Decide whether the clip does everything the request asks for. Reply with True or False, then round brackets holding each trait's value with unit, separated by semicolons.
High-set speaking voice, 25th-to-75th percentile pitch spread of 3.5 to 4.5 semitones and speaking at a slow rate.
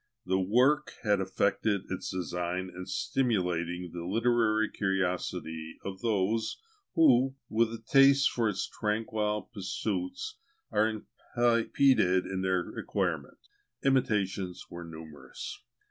False (105 Hz; 4.2 semitones; 110 wpm)